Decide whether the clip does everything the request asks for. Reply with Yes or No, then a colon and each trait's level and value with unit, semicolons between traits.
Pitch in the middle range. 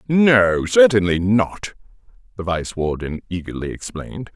No: low, 100 Hz